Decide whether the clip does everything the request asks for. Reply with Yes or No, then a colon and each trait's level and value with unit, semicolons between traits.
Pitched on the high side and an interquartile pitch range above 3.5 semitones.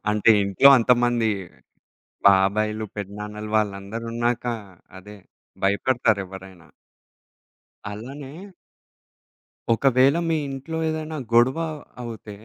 No: low, 110 Hz; average, 4.0 semitones